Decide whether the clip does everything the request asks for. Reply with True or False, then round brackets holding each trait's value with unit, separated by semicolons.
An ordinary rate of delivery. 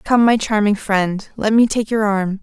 False (225 wpm)